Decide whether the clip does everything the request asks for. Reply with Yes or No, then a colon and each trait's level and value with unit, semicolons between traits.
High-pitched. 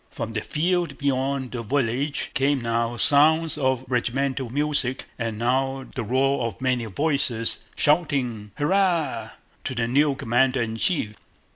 No: low, 130 Hz